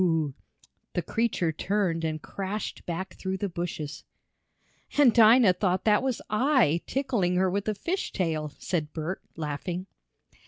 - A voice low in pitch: No, medium, 185 Hz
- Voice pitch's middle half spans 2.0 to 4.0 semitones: No, average, 4.5 semitones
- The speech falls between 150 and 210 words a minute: No, average, 140 wpm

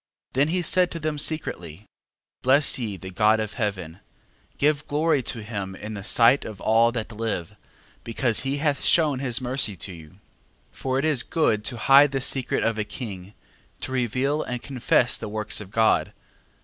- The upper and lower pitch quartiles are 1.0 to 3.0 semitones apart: No, average, 4.8 semitones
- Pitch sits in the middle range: No, low, 120 Hz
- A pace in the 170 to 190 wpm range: Yes, average, 185 wpm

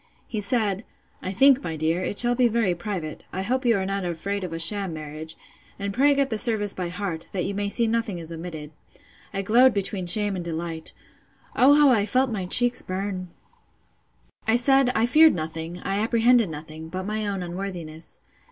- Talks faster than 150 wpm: Yes, average, 195 wpm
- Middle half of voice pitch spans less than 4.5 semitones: No, average, 5.1 semitones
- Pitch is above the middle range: Yes, high, 195 Hz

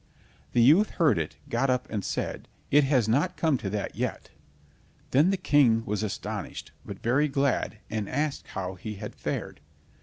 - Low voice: Yes, low, 125 Hz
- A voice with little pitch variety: No, wide, 5.5 semitones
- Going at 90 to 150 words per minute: No, average, 175 wpm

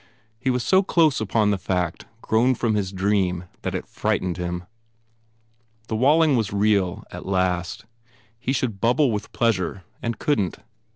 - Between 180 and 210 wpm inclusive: No, average, 160 wpm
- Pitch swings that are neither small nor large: Yes, average, 4.9 semitones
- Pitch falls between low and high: No, low, 105 Hz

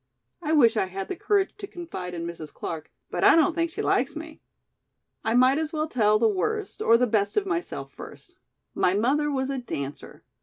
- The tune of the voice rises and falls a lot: Yes, wide, 8.7 semitones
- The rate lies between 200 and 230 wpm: Yes, fast, 205 wpm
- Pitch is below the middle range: No, very high, 255 Hz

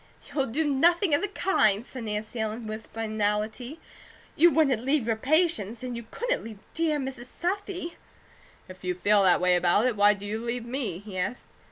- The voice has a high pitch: Yes, high, 235 Hz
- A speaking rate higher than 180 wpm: Yes, average, 190 wpm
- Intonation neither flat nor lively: No, wide, 6.0 semitones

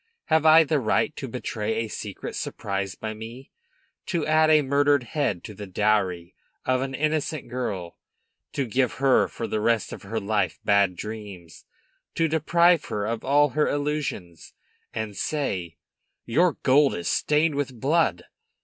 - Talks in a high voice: No, low, 120 Hz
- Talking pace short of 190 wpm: Yes, average, 160 wpm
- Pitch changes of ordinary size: No, wide, 6.3 semitones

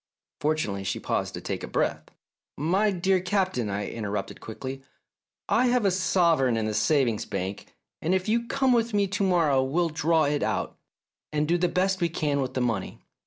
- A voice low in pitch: No, medium, 160 Hz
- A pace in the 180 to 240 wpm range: Yes, average, 190 wpm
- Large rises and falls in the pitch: Yes, wide, 6.9 semitones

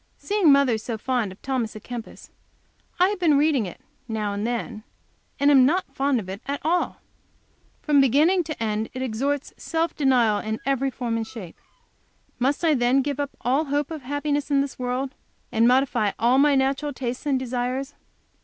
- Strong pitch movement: No, average, 3.4 semitones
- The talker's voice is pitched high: Yes, very high, 265 Hz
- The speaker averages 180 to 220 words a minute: Yes, average, 190 wpm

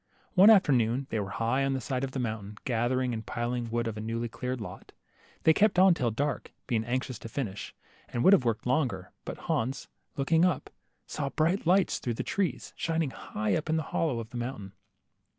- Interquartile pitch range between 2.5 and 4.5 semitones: No, average, 5.0 semitones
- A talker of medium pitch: No, low, 125 Hz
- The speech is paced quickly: Yes, fast, 210 wpm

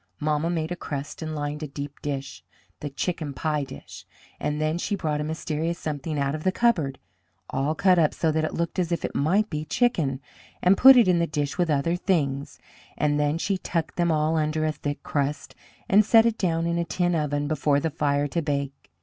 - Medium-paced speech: No, fast, 220 wpm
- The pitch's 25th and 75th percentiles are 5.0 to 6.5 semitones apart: No, average, 2.7 semitones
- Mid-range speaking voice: Yes, medium, 155 Hz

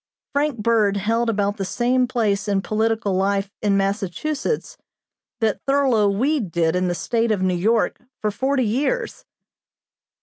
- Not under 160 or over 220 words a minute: No, average, 145 wpm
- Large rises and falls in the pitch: No, average, 3.7 semitones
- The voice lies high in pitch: Yes, high, 215 Hz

